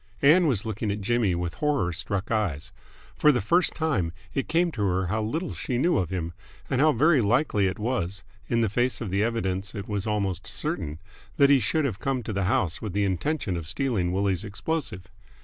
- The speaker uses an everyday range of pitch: No, wide, 5.9 semitones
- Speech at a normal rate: No, fast, 210 wpm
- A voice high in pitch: No, low, 105 Hz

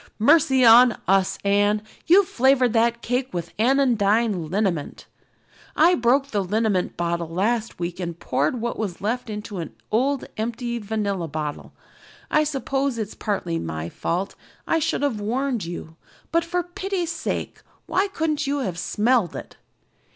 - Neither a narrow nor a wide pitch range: No, wide, 6.2 semitones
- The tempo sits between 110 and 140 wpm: No, average, 150 wpm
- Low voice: No, high, 225 Hz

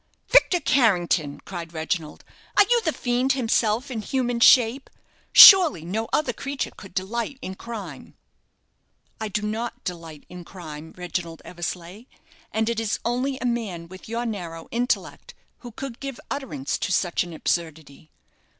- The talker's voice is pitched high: Yes, high, 215 Hz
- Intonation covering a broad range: Yes, wide, 6.1 semitones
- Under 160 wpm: Yes, average, 150 wpm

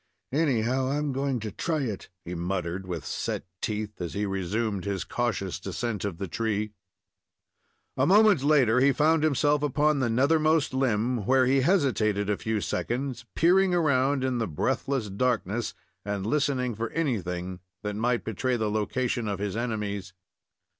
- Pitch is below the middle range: Yes, low, 120 Hz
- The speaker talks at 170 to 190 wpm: No, average, 160 wpm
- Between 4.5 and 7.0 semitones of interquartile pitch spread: Yes, average, 5.1 semitones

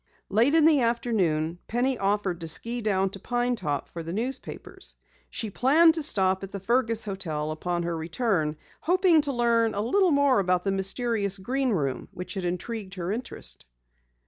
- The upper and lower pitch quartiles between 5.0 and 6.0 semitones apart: Yes, average, 5.3 semitones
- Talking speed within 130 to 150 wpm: No, average, 175 wpm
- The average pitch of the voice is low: No, high, 205 Hz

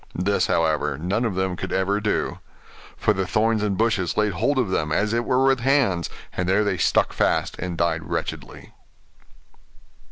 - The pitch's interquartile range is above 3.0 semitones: Yes, average, 4.1 semitones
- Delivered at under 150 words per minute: No, average, 180 wpm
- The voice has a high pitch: No, low, 100 Hz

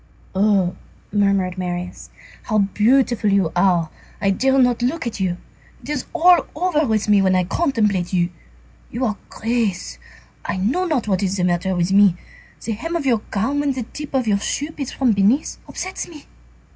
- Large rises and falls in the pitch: Yes, wide, 5.9 semitones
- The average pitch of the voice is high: Yes, high, 210 Hz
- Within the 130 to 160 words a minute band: No, average, 185 wpm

